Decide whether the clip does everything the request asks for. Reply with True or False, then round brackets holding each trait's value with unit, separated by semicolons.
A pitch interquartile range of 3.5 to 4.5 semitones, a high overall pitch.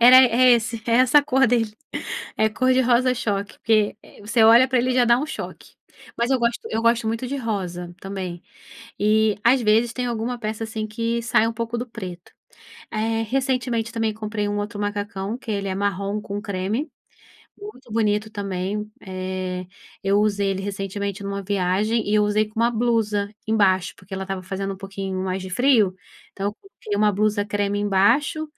False (2.9 semitones; 215 Hz)